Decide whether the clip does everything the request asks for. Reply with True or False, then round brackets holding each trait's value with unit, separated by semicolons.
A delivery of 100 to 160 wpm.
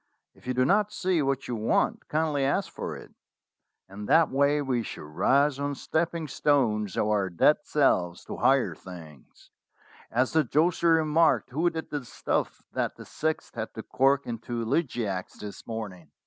False (170 wpm)